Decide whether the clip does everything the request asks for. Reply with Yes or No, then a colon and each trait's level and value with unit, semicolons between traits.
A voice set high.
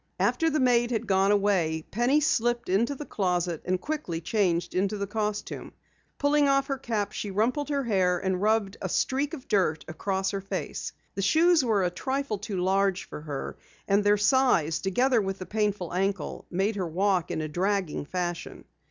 Yes: high, 200 Hz